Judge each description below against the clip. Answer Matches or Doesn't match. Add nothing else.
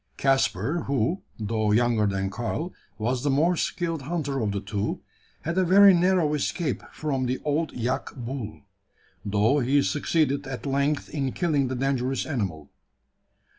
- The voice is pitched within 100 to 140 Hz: Matches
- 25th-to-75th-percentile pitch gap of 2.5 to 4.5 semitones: Doesn't match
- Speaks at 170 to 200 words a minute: Doesn't match